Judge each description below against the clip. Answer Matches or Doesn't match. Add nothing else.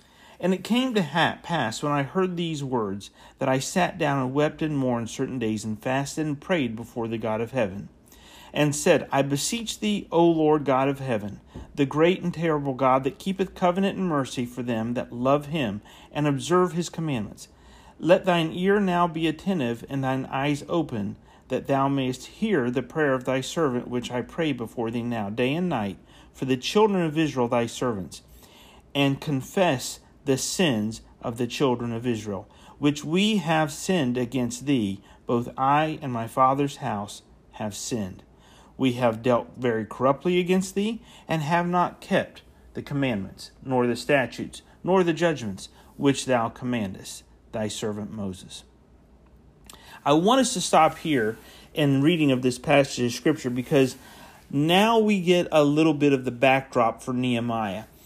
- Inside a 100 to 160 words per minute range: Doesn't match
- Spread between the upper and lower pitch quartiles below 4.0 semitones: Doesn't match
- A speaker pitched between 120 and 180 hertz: Matches